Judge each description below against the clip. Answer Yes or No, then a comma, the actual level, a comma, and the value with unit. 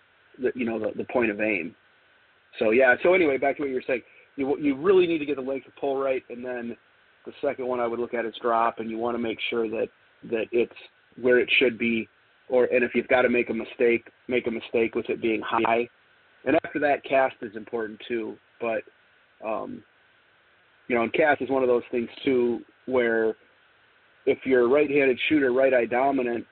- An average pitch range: No, wide, 7.6 semitones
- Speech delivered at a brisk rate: Yes, fast, 220 wpm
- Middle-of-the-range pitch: No, low, 125 Hz